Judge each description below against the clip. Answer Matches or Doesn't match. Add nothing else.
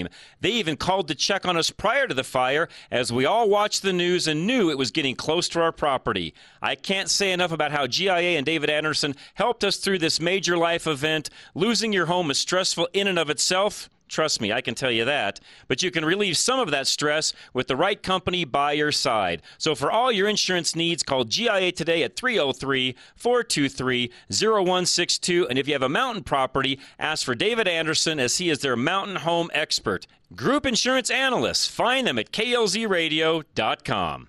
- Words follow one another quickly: Doesn't match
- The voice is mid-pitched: Matches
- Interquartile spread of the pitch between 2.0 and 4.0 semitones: Doesn't match